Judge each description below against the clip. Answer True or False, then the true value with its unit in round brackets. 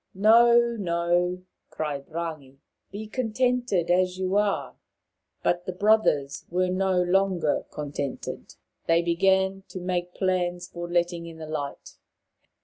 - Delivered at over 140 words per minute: False (135 wpm)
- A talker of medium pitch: True (180 Hz)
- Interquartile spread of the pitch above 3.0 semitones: False (2.4 semitones)